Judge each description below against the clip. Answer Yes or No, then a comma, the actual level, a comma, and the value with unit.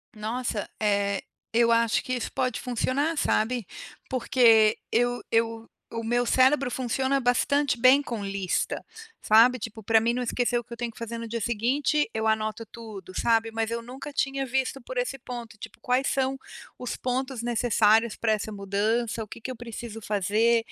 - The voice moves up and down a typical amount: No, narrow, 2.3 semitones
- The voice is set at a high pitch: Yes, high, 235 Hz